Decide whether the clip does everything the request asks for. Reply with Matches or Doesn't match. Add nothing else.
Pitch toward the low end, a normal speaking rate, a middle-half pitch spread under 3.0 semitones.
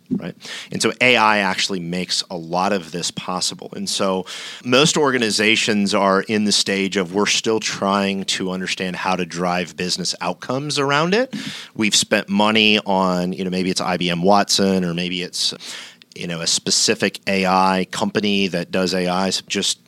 Matches